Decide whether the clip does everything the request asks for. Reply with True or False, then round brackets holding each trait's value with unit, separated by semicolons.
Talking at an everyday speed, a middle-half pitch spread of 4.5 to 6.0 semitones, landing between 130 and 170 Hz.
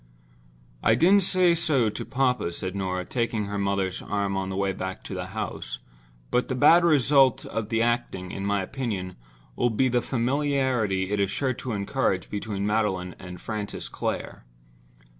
False (170 wpm; 5.1 semitones; 105 Hz)